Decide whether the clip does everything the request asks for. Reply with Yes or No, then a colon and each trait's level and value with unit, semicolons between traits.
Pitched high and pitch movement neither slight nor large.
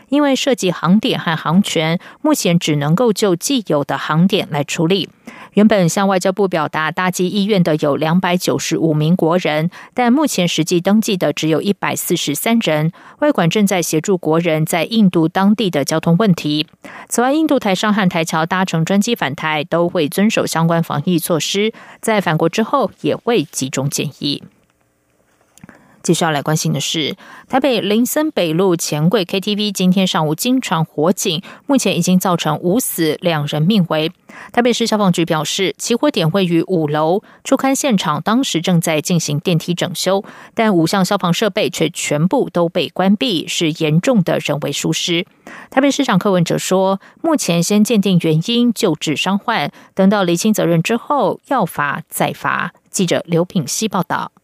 No: medium, 180 Hz; average, 4.7 semitones